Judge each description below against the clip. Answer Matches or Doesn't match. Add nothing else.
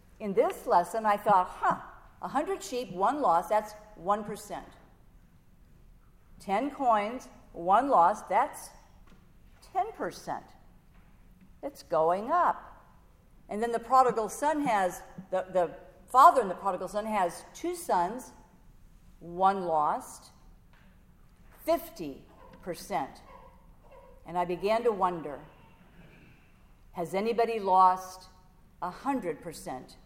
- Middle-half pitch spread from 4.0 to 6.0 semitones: Matches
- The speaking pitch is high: Matches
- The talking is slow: Matches